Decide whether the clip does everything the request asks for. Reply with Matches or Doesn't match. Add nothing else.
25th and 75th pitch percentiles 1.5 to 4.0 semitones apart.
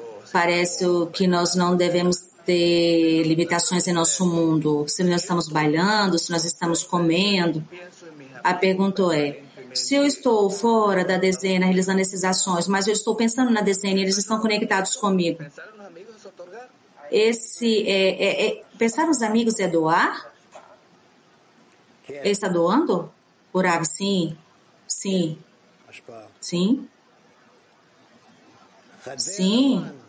Matches